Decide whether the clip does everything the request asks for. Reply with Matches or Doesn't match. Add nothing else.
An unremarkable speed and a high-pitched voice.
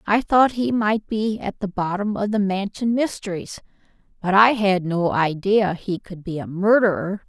Matches